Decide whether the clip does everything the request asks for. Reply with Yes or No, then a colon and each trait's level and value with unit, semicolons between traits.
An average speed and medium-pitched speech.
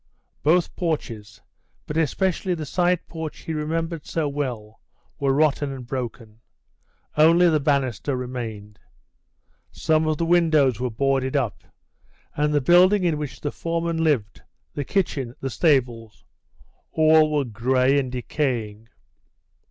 No: slow, 130 wpm; medium, 145 Hz